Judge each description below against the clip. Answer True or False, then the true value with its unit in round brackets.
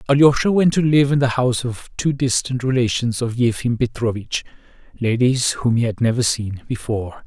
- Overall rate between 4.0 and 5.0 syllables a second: False (5.3 syllables/s)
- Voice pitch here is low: True (125 Hz)